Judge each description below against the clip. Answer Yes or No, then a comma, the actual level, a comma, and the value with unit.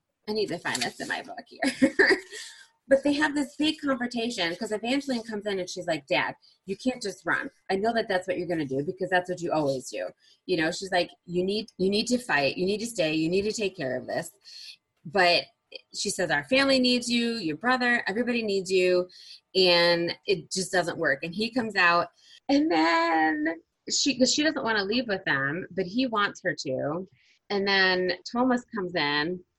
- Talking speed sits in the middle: No, fast, 210 wpm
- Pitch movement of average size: No, wide, 5.8 semitones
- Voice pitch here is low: No, high, 195 Hz